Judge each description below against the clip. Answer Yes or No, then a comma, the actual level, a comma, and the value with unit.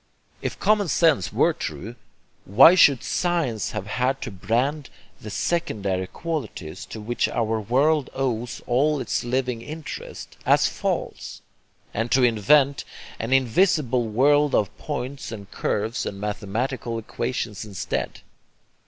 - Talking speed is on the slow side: Yes, slow, 125 wpm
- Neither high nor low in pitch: No, low, 125 Hz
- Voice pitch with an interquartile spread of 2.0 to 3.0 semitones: No, average, 5.1 semitones